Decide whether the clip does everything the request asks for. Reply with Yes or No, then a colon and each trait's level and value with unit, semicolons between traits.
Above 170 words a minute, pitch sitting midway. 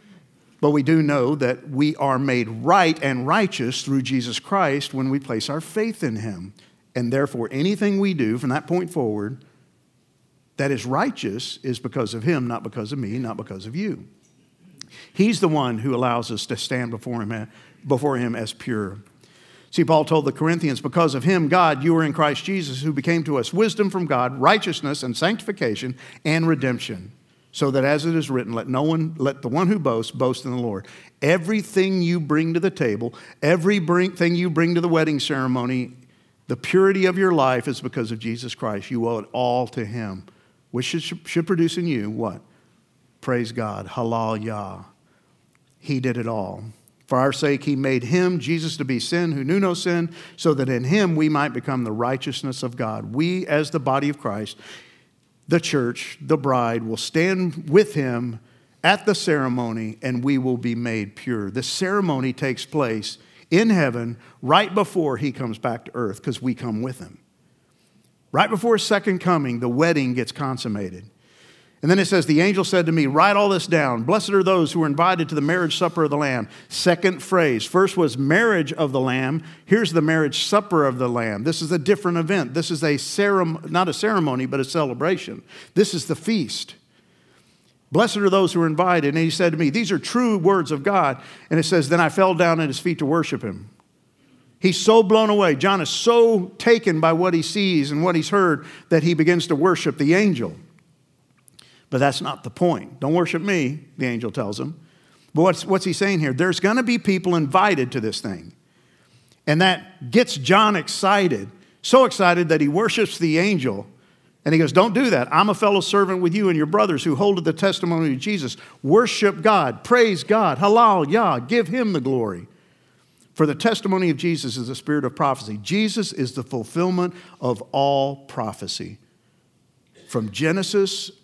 Yes: average, 195 wpm; medium, 155 Hz